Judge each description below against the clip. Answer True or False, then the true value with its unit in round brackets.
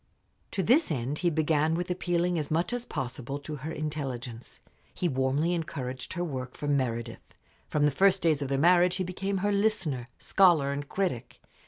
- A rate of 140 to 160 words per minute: False (180 wpm)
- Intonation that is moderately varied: True (4.7 semitones)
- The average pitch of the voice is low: False (155 Hz)